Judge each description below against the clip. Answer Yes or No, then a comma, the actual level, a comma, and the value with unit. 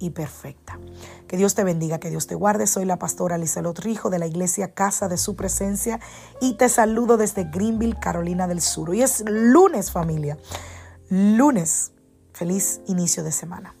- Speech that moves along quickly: No, average, 170 wpm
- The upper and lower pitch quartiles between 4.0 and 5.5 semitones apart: Yes, average, 4.3 semitones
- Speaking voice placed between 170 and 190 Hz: Yes, medium, 185 Hz